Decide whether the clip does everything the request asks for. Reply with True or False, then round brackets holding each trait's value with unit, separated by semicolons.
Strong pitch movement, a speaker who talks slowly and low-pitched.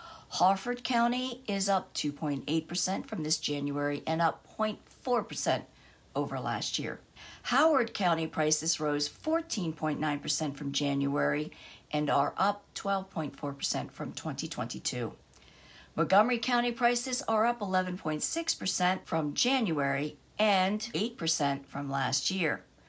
False (6.7 semitones; 105 wpm; 165 Hz)